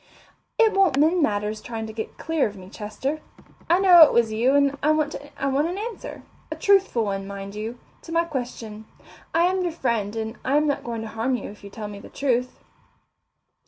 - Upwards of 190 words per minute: Yes, fast, 205 wpm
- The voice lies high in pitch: Yes, very high, 255 Hz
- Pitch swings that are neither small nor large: No, wide, 6.4 semitones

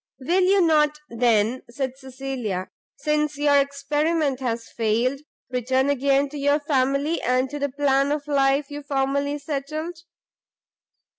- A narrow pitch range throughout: Yes, narrow, 2.1 semitones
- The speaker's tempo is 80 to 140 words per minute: Yes, slow, 135 wpm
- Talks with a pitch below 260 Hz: No, very high, 280 Hz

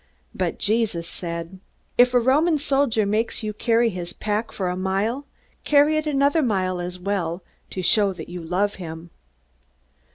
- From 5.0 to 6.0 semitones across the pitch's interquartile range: Yes, wide, 5.4 semitones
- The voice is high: Yes, high, 205 Hz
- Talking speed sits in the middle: Yes, average, 160 wpm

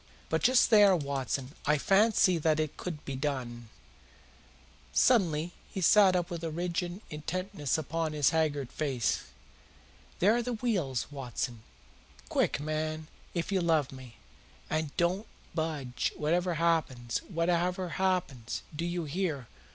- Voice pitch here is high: No, medium, 160 Hz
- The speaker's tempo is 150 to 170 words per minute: No, slow, 135 wpm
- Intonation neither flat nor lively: Yes, average, 4.2 semitones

